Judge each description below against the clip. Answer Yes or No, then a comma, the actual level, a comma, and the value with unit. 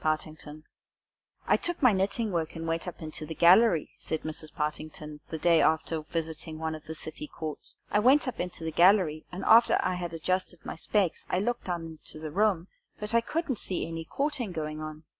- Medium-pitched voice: Yes, medium, 165 Hz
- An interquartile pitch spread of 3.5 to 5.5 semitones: Yes, average, 3.9 semitones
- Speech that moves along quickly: Yes, fast, 210 wpm